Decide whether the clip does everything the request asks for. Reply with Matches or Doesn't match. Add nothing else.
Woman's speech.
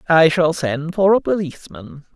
Doesn't match